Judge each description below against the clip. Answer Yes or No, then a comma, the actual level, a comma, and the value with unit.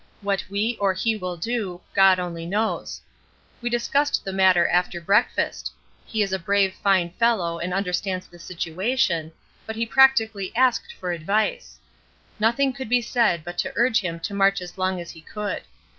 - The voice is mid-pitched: No, high, 195 Hz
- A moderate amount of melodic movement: Yes, average, 4.1 semitones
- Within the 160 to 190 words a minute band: Yes, average, 175 wpm